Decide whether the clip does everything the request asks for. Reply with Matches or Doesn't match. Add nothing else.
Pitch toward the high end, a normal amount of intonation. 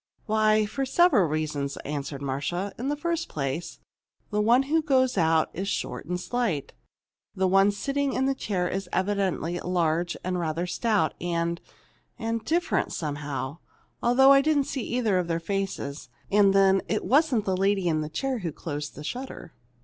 Doesn't match